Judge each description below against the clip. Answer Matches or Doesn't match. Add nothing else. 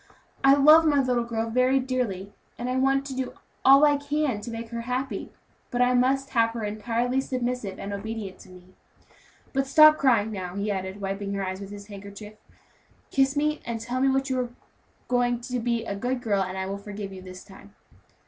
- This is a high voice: Matches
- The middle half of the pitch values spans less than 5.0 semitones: Matches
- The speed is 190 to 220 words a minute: Matches